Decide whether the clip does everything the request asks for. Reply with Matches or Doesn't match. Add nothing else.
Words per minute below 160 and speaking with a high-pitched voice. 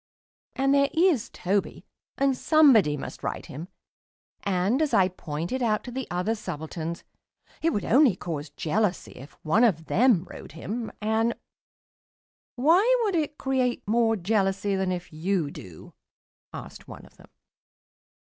Matches